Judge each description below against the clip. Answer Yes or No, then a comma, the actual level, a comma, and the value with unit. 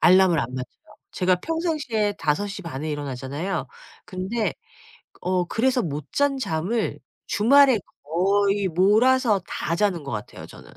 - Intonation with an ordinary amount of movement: No, wide, 5.9 semitones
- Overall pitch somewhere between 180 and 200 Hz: Yes, high, 190 Hz